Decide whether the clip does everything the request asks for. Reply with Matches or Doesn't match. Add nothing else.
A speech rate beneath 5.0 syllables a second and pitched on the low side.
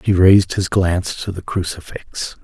Matches